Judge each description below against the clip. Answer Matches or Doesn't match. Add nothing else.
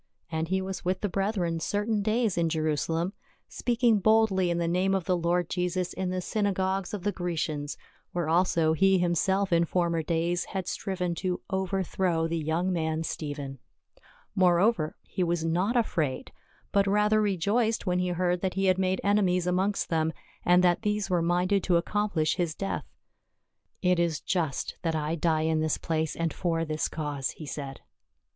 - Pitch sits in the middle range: Matches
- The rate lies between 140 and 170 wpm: Doesn't match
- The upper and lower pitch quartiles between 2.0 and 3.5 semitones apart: Matches